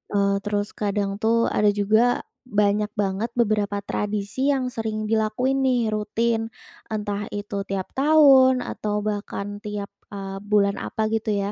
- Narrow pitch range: Yes, narrow, 2.0 semitones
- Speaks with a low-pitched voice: No, high, 210 Hz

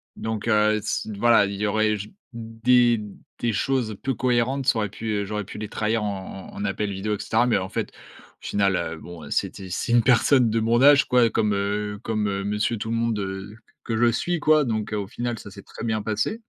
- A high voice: No, low, 110 Hz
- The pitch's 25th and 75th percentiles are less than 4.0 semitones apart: Yes, narrow, 2.5 semitones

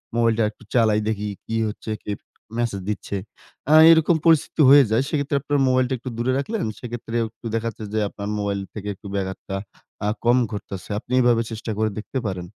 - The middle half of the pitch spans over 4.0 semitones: No, average, 3.6 semitones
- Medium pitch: No, low, 115 Hz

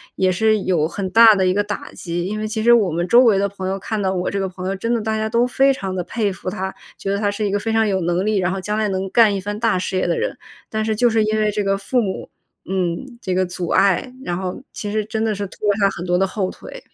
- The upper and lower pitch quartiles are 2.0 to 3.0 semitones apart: Yes, narrow, 2.6 semitones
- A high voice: Yes, high, 200 Hz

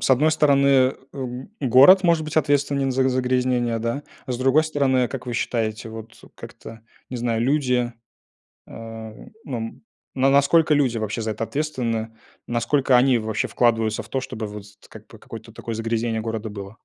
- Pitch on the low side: Yes, low, 125 Hz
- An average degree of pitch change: Yes, average, 3.3 semitones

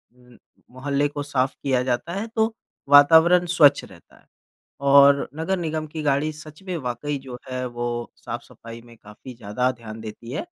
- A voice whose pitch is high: No, medium, 140 Hz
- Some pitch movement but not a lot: Yes, average, 4.1 semitones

